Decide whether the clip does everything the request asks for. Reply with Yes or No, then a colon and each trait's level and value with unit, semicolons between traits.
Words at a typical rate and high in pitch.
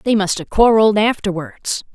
Yes: average, 155 wpm; high, 205 Hz